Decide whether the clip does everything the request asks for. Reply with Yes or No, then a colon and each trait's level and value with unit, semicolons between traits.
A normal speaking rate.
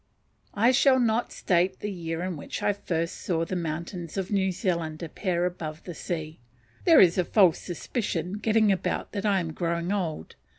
Yes: average, 180 wpm